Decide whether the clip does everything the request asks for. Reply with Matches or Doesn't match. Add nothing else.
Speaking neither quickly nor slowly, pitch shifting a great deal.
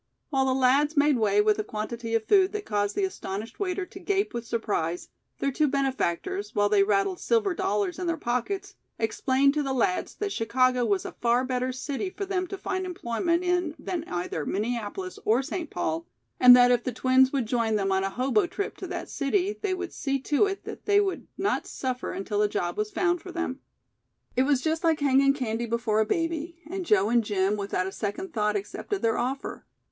Doesn't match